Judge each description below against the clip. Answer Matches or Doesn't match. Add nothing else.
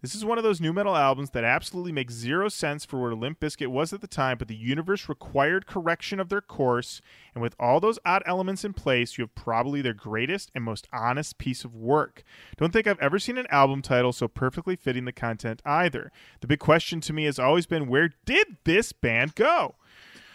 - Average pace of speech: Doesn't match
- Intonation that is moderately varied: Doesn't match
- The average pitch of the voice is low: Doesn't match